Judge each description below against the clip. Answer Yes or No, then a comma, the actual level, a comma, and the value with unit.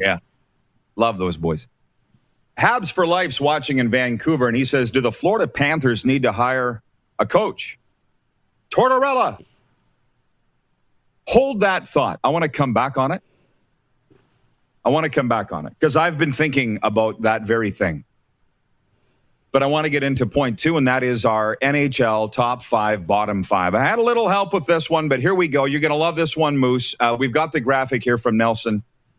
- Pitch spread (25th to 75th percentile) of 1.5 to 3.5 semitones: No, average, 5.1 semitones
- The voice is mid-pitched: No, low, 130 Hz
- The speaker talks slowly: No, average, 190 wpm